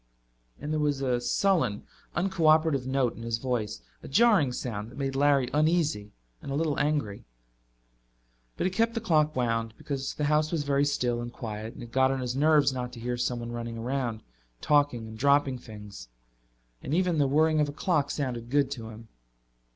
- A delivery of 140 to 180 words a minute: No, average, 190 wpm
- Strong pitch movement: No, average, 4.2 semitones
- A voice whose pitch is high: No, low, 135 Hz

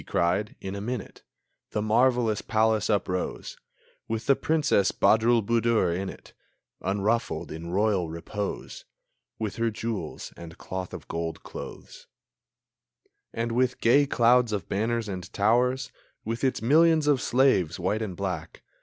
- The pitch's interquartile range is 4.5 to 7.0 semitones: No, average, 3.8 semitones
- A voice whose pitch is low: Yes, low, 110 Hz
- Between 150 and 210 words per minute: No, slow, 135 wpm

